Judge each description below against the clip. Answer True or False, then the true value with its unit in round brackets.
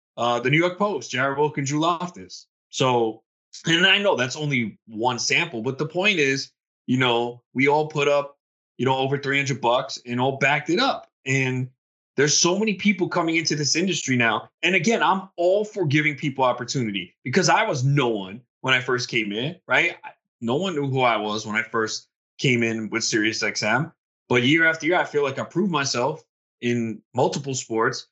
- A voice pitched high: False (135 Hz)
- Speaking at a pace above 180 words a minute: True (200 wpm)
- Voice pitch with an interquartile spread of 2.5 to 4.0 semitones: False (5.1 semitones)